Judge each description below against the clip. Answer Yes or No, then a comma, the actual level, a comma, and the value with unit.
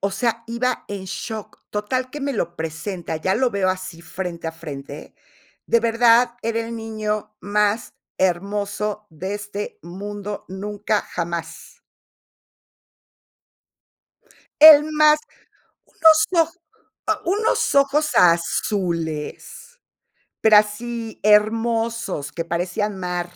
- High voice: Yes, high, 210 Hz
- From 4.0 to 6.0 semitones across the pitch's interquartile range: Yes, average, 4.6 semitones